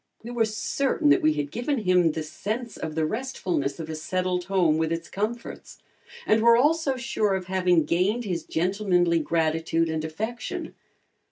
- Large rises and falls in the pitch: Yes, wide, 5.8 semitones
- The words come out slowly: No, average, 170 wpm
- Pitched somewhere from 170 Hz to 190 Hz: Yes, medium, 185 Hz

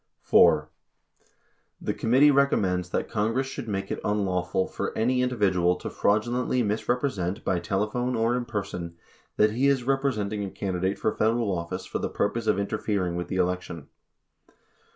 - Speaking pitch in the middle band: No, low, 105 Hz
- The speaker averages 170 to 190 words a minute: No, average, 150 wpm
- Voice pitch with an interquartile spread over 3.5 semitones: Yes, average, 4.7 semitones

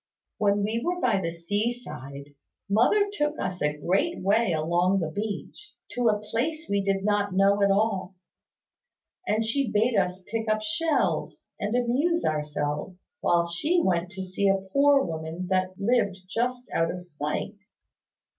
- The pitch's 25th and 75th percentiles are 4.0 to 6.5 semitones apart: Yes, average, 4.6 semitones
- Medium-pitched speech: No, high, 200 Hz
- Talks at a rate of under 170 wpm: Yes, average, 160 wpm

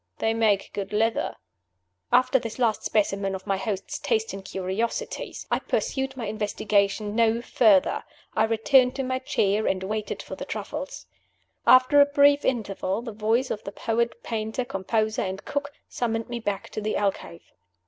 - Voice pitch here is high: Yes, high, 220 Hz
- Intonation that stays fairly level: No, average, 3.5 semitones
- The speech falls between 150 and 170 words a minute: Yes, average, 165 wpm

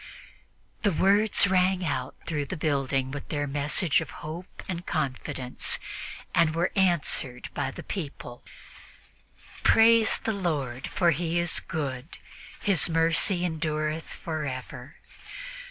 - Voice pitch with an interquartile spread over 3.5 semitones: Yes, average, 4.2 semitones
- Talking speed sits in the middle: No, slow, 120 wpm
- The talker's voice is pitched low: No, medium, 160 Hz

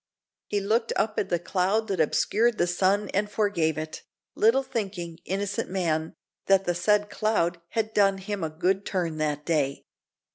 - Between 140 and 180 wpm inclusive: Yes, average, 170 wpm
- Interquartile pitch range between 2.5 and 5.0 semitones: Yes, average, 3.5 semitones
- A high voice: Yes, high, 195 Hz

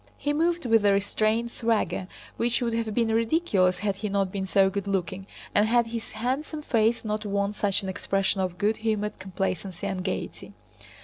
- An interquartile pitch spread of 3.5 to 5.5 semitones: No, average, 2.8 semitones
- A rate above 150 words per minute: Yes, average, 185 wpm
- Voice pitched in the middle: No, high, 210 Hz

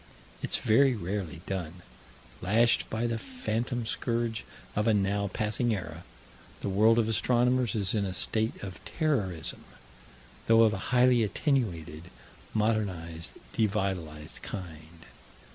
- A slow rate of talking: Yes, slow, 125 wpm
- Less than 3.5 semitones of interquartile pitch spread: No, average, 4.2 semitones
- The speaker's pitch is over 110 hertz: No, low, 105 Hz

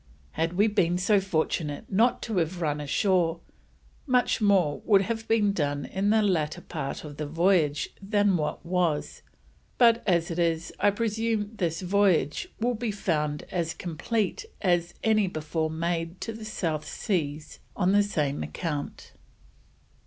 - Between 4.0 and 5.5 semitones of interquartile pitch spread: Yes, average, 4.4 semitones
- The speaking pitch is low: No, medium, 180 Hz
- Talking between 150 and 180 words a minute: Yes, average, 155 wpm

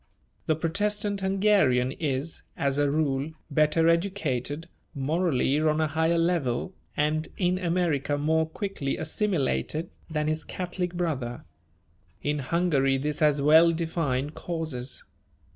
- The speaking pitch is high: No, medium, 155 Hz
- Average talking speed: No, slow, 120 wpm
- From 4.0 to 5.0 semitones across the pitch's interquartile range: No, average, 3.3 semitones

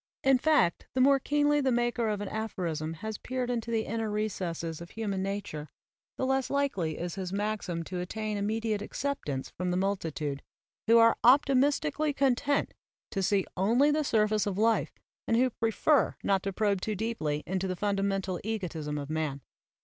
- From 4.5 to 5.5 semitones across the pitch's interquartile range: Yes, average, 4.9 semitones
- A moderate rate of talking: Yes, average, 170 wpm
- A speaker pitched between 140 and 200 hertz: No, high, 210 Hz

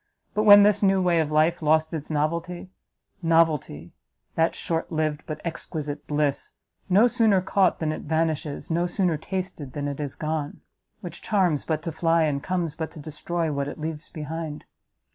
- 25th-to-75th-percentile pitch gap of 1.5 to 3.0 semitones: Yes, narrow, 2.6 semitones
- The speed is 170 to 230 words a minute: Yes, average, 175 wpm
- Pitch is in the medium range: Yes, medium, 160 Hz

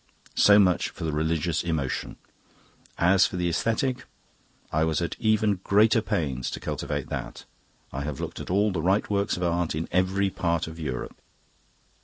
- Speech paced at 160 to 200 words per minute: Yes, average, 170 wpm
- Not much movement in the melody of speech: No, average, 3.8 semitones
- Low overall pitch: Yes, very low, 90 Hz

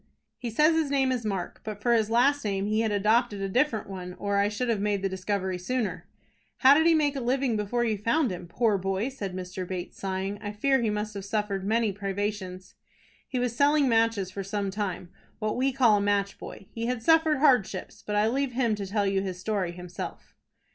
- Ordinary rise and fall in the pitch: Yes, average, 4.0 semitones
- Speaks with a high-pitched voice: Yes, high, 210 Hz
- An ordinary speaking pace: No, fast, 220 wpm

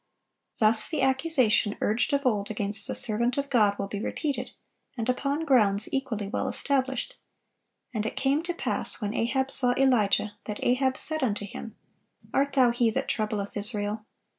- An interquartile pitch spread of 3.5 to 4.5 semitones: Yes, average, 4.2 semitones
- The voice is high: Yes, high, 235 Hz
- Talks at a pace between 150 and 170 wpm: Yes, average, 165 wpm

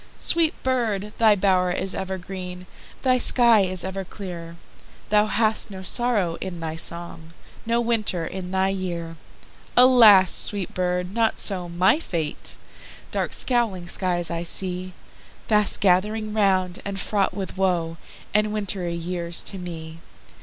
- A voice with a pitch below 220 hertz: Yes, high, 190 Hz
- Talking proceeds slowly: Yes, slow, 120 wpm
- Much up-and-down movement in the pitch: No, average, 3.2 semitones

